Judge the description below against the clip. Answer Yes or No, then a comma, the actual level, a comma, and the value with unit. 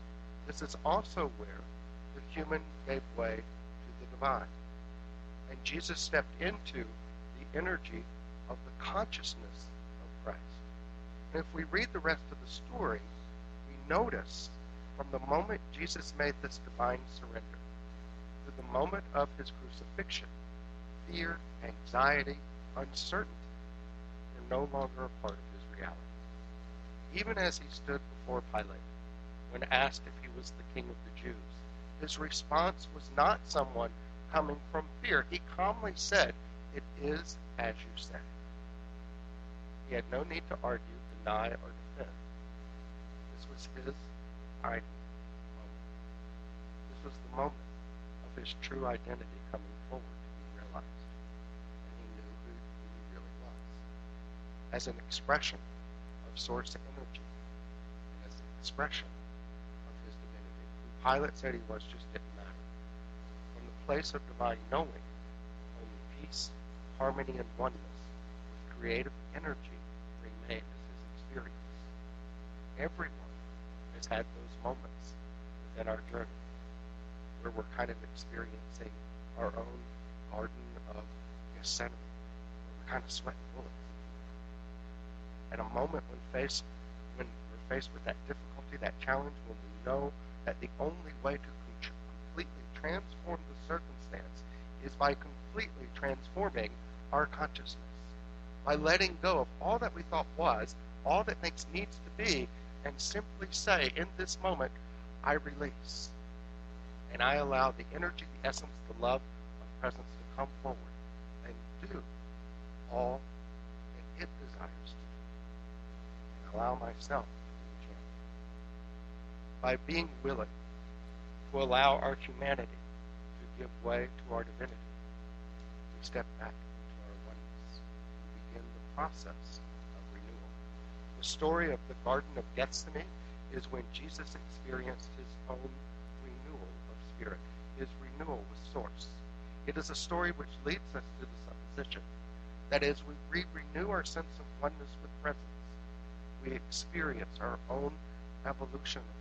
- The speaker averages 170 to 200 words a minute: No, slow, 135 wpm